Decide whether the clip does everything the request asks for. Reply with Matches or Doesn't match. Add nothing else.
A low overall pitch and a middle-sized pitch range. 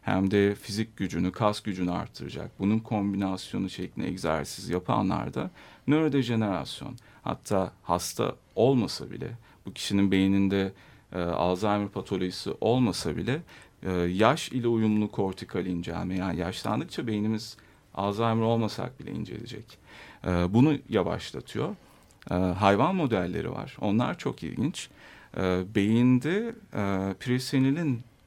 Matches